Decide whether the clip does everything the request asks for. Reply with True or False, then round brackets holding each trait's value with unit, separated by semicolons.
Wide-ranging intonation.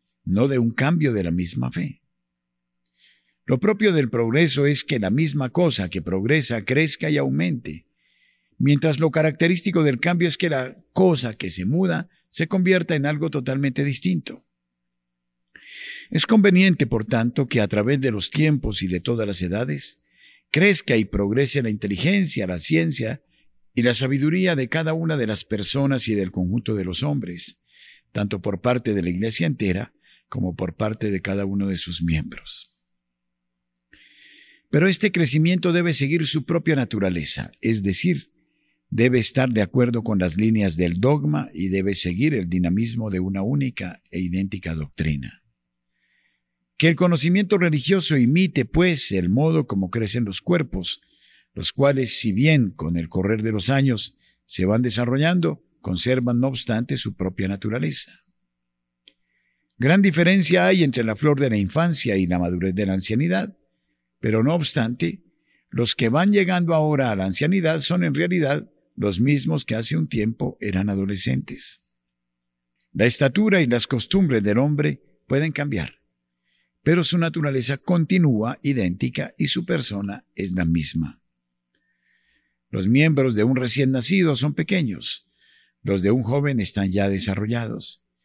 True (8.8 semitones)